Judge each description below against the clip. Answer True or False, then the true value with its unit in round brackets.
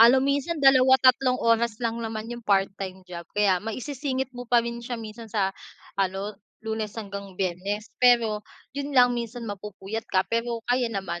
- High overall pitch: True (225 Hz)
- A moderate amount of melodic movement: True (3.5 semitones)